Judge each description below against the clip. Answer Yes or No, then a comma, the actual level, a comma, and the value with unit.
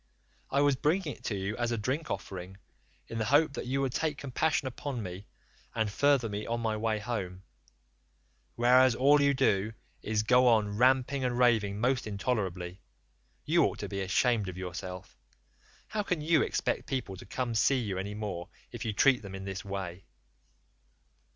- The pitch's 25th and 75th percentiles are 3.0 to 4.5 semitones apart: No, average, 4.9 semitones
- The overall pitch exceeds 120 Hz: No, low, 115 Hz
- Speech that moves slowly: No, average, 185 wpm